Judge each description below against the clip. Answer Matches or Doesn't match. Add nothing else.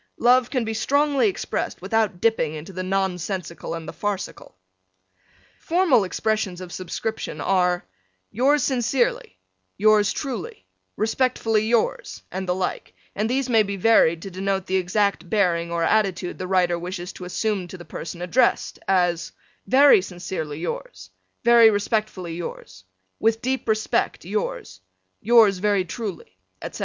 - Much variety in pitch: Doesn't match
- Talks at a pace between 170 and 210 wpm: Doesn't match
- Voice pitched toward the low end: Doesn't match